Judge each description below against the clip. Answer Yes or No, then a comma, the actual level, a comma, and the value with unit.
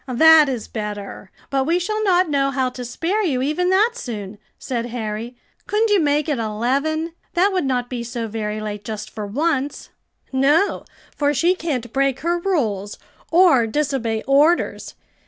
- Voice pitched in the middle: No, very high, 270 Hz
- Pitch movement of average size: No, wide, 6.2 semitones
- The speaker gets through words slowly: No, average, 165 wpm